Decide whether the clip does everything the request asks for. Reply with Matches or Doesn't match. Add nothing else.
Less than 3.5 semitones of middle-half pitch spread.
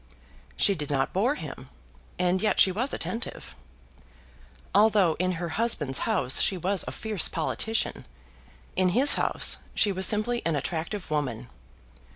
Doesn't match